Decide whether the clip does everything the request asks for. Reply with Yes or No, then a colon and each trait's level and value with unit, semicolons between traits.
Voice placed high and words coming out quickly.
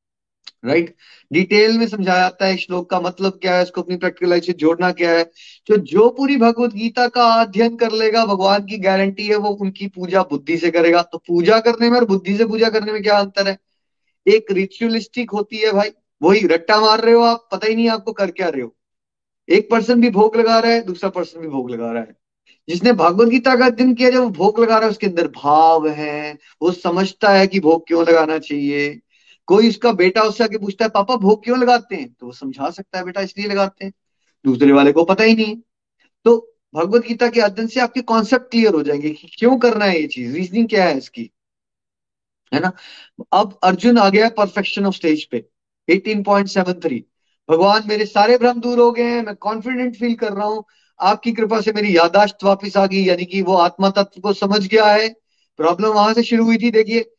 Yes: high, 200 Hz; fast, 215 wpm